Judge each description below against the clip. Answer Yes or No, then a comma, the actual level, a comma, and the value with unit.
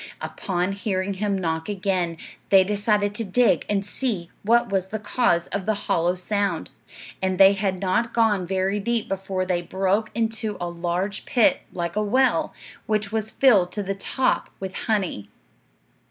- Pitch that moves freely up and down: No, narrow, 2.5 semitones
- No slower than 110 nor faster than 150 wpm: No, average, 165 wpm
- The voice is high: Yes, high, 195 Hz